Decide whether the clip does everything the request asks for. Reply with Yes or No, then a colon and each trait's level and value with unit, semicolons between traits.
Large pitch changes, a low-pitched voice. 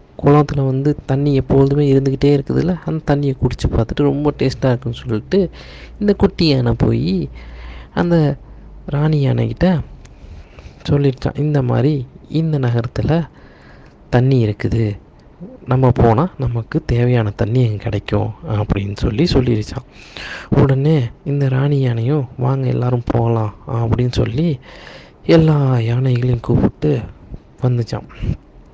No: average, 3.8 semitones; low, 130 Hz